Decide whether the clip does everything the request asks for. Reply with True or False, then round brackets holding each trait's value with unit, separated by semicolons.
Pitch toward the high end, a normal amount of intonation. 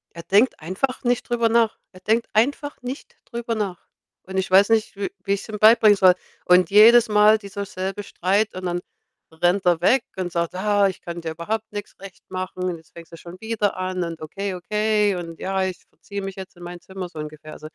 True (195 Hz; 3.2 semitones)